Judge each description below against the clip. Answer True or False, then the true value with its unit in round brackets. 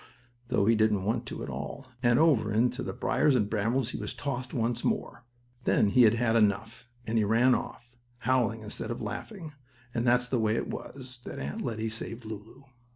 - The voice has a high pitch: False (115 Hz)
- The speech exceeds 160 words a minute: True (200 wpm)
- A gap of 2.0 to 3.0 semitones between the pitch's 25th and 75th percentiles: True (2.4 semitones)